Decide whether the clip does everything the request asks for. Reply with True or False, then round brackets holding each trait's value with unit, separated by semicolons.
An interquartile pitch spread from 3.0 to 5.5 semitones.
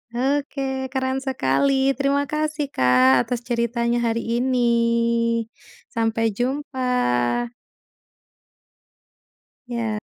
False (2.5 semitones)